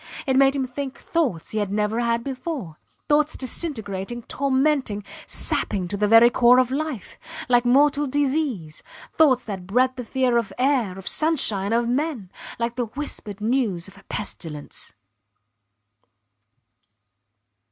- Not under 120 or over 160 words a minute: Yes, average, 140 wpm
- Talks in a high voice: Yes, high, 245 Hz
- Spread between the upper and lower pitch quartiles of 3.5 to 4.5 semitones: No, average, 4.9 semitones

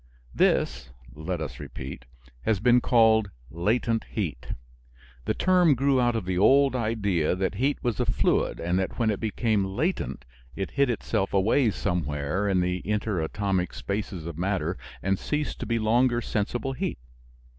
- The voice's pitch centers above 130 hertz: No, low, 105 Hz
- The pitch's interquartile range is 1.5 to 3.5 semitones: No, average, 4.8 semitones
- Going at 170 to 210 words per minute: No, average, 155 wpm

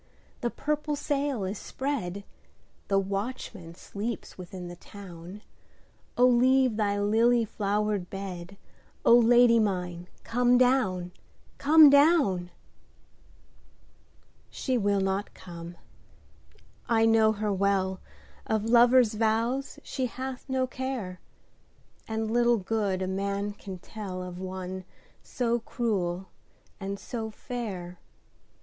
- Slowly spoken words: Yes, slow, 95 wpm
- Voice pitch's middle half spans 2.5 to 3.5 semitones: No, average, 4.4 semitones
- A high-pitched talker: Yes, high, 210 Hz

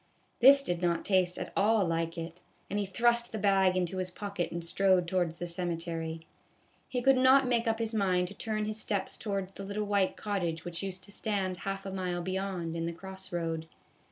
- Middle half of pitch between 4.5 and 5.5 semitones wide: No, average, 3.0 semitones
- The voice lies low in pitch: No, high, 190 Hz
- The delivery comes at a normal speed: No, fast, 210 wpm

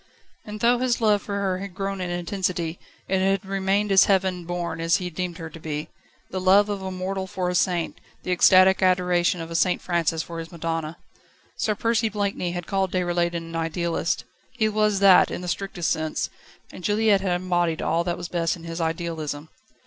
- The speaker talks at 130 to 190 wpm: No, average, 200 wpm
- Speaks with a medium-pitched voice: Yes, medium, 180 Hz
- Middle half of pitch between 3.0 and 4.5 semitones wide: No, narrow, 2.5 semitones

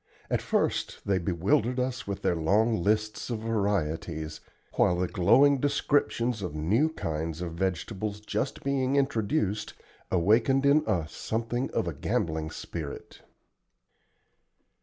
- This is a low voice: Yes, low, 105 Hz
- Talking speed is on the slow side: Yes, slow, 125 wpm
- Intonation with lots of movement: Yes, wide, 6.3 semitones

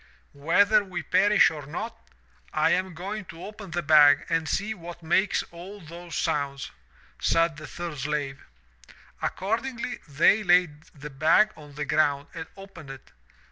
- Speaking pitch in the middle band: Yes, medium, 165 Hz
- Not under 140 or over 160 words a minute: Yes, average, 150 wpm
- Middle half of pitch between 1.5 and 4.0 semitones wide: No, average, 4.6 semitones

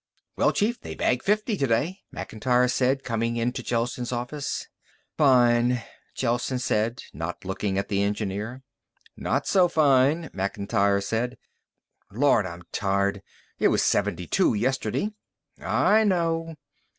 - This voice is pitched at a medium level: No, low, 120 Hz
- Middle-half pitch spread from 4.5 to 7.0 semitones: Yes, average, 5.0 semitones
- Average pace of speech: No, slow, 125 wpm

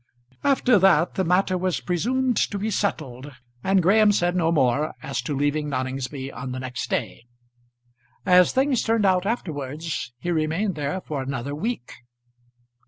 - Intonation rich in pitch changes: Yes, wide, 6.1 semitones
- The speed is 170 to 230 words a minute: No, average, 155 wpm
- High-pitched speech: No, medium, 165 Hz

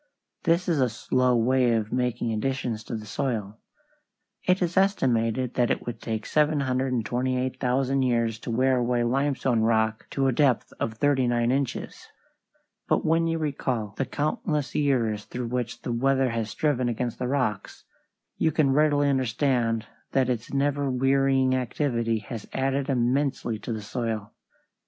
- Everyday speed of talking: Yes, average, 150 wpm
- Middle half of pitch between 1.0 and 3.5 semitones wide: Yes, average, 2.9 semitones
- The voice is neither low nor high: No, low, 125 Hz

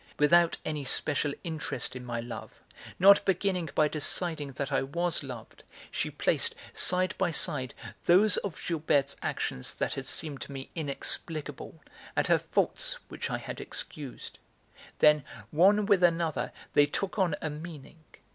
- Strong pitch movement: No, average, 3.8 semitones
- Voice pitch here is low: No, medium, 155 Hz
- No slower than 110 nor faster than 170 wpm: Yes, average, 150 wpm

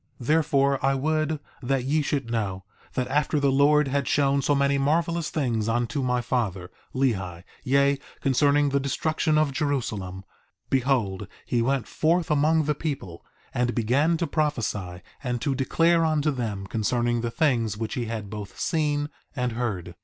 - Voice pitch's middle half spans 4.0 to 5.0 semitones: Yes, average, 4.3 semitones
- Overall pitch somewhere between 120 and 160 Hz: Yes, low, 135 Hz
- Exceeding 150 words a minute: Yes, average, 160 wpm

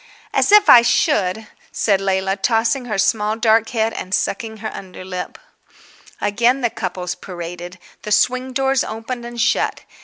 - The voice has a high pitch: Yes, high, 220 Hz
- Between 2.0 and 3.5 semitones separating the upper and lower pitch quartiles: No, average, 3.9 semitones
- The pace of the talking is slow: No, average, 150 wpm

